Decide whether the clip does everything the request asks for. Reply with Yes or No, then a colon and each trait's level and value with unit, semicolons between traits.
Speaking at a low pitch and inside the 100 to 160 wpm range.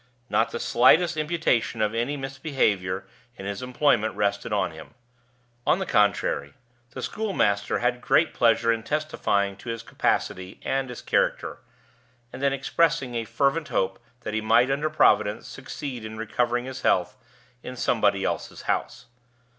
Yes: low, 120 Hz; average, 150 wpm